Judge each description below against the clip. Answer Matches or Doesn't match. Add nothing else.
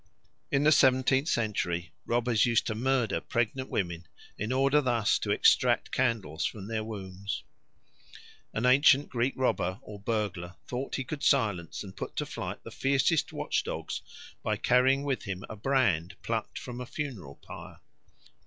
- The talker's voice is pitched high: Doesn't match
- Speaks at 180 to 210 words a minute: Doesn't match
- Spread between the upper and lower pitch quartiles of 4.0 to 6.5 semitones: Matches